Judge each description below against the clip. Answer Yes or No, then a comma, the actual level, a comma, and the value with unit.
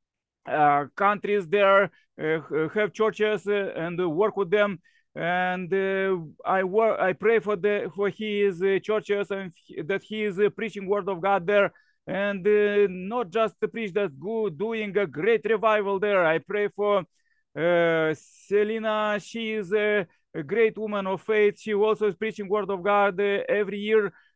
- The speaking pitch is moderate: No, high, 205 Hz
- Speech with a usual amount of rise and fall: No, narrow, 1.8 semitones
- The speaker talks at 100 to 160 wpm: No, average, 170 wpm